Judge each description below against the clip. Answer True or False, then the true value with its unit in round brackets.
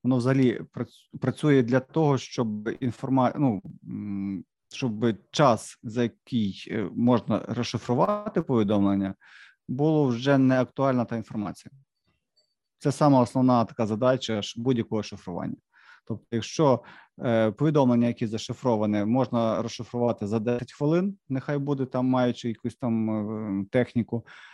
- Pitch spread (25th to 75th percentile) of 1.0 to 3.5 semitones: True (2.9 semitones)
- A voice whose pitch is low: True (120 Hz)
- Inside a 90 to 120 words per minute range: True (110 wpm)